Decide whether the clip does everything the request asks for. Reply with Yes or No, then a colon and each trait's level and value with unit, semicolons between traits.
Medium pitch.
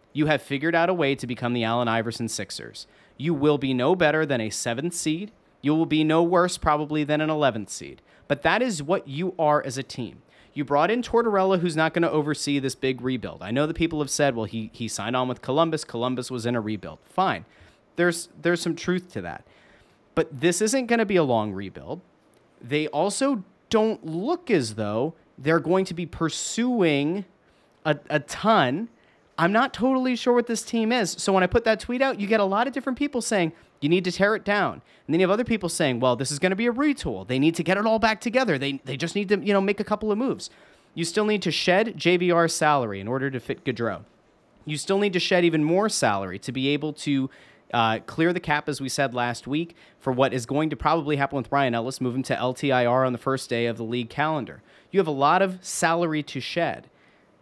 Yes: medium, 155 Hz